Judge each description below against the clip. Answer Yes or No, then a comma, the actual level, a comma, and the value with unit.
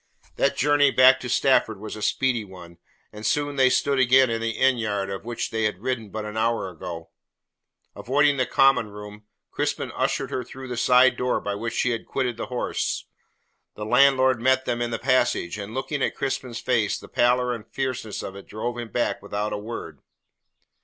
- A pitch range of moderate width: Yes, average, 3.5 semitones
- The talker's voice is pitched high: No, low, 120 Hz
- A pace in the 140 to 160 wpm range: No, average, 200 wpm